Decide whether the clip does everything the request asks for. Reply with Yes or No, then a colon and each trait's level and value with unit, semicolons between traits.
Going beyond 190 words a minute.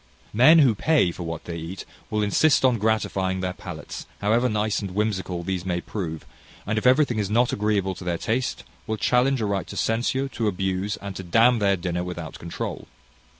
Yes: average, 200 wpm